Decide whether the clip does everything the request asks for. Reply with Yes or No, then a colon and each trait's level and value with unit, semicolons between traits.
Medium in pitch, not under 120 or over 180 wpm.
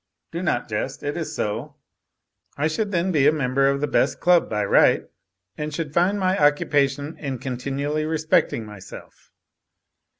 Yes: medium, 145 Hz; average, 160 wpm